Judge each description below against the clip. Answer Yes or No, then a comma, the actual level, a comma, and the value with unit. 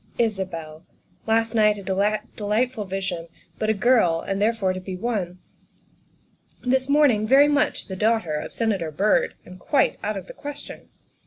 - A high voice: Yes, high, 210 Hz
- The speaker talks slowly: No, average, 155 wpm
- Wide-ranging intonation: No, average, 3.8 semitones